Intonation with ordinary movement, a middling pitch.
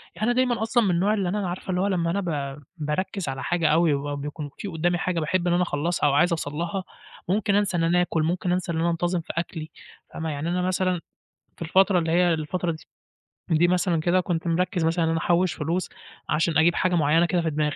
No: narrow, 2.3 semitones; medium, 175 Hz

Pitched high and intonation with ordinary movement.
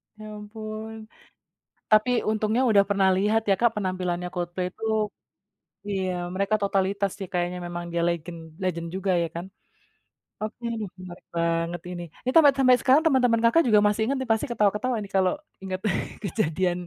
Yes: high, 200 Hz; average, 3.5 semitones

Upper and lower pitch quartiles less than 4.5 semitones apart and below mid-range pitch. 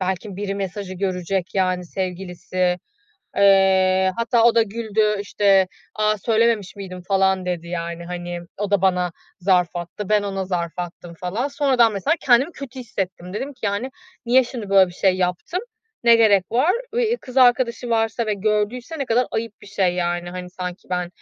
No: average, 4.1 semitones; high, 195 Hz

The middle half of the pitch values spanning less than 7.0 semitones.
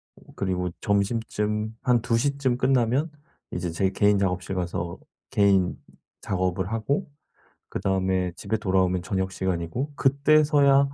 Yes: average, 5.2 semitones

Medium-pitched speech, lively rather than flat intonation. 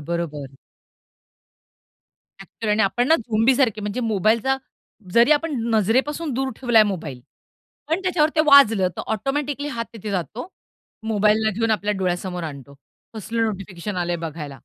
No: high, 220 Hz; wide, 6.1 semitones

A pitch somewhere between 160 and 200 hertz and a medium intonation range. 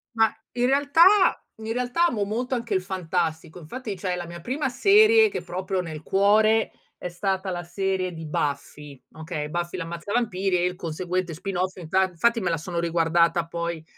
Yes: medium, 185 Hz; average, 4.5 semitones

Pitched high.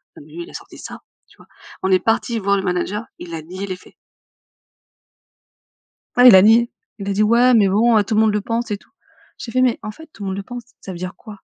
Yes: high, 205 Hz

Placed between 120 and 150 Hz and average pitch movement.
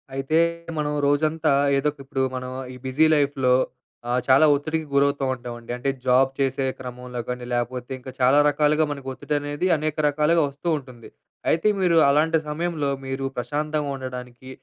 Yes: medium, 140 Hz; average, 3.0 semitones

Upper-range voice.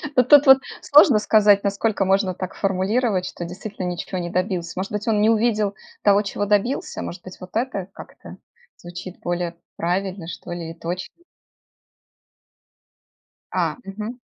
Yes: high, 195 Hz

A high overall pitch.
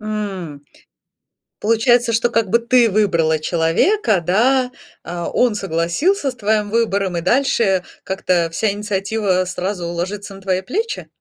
Yes: high, 205 Hz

